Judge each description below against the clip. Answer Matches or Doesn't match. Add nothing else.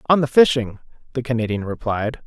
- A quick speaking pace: Doesn't match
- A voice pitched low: Matches